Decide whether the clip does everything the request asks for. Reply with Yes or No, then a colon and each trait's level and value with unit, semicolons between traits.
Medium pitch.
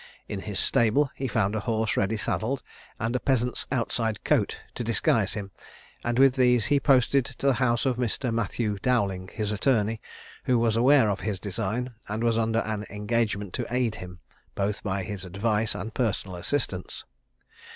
No: low, 110 Hz